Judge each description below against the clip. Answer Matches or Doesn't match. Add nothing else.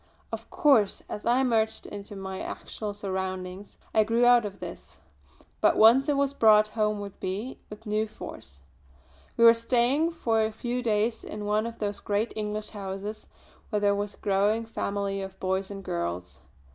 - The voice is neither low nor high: Doesn't match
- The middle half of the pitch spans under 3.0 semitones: Matches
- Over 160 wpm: Matches